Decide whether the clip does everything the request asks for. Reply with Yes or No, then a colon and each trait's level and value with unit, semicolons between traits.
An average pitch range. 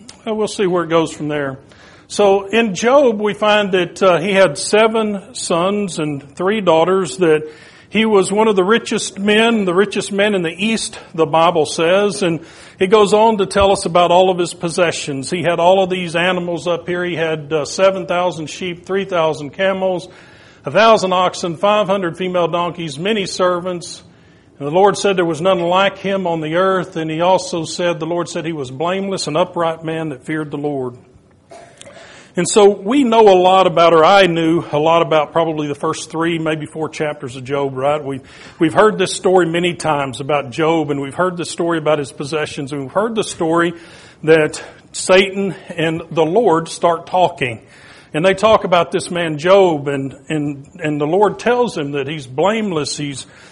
Yes: average, 3.7 semitones